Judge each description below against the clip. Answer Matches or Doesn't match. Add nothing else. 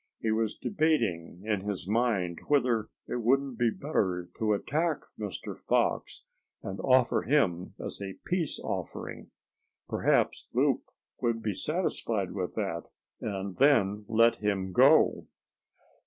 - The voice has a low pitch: Matches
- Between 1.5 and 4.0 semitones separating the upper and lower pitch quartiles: Doesn't match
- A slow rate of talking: Matches